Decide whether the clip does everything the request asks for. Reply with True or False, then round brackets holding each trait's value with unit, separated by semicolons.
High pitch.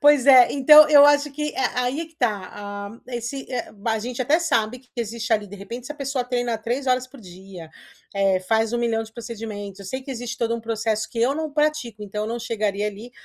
True (235 Hz)